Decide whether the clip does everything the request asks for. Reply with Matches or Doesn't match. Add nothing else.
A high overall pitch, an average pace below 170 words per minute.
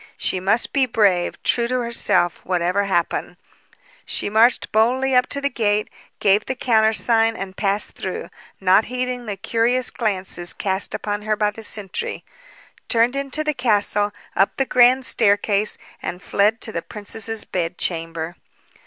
Matches